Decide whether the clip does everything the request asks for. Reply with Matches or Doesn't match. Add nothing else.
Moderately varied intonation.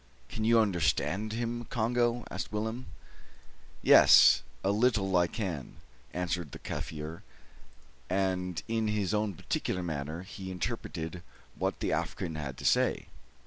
Matches